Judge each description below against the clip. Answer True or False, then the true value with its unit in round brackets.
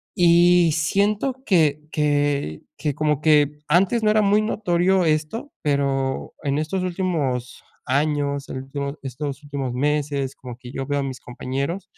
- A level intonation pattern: False (4.1 semitones)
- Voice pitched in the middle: True (150 Hz)